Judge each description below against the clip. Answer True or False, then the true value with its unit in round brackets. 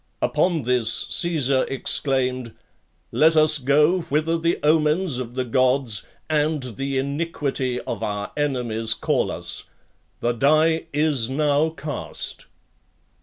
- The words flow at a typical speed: False (120 wpm)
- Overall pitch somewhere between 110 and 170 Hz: True (140 Hz)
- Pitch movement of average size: True (3.6 semitones)